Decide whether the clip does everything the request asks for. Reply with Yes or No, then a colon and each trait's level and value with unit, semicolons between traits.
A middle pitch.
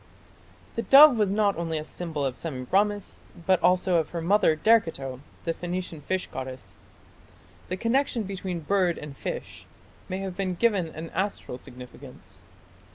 Yes: medium, 180 Hz